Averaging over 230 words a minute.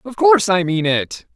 No: fast, 220 wpm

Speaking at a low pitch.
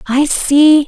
No: very high, 290 Hz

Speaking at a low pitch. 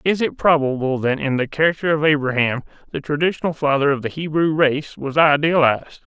No: medium, 145 Hz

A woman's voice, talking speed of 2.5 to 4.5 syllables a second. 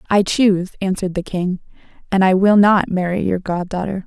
No: female; 5.6 syllables/s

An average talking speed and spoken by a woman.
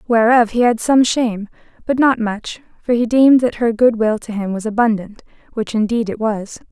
Yes: average, 195 wpm; female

